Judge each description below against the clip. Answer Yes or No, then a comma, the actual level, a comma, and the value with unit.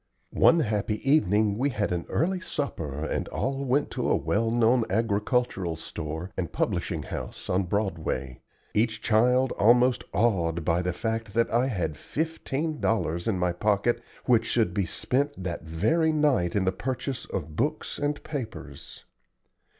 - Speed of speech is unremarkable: Yes, average, 155 wpm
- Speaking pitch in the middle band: No, low, 110 Hz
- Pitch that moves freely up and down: Yes, wide, 6.3 semitones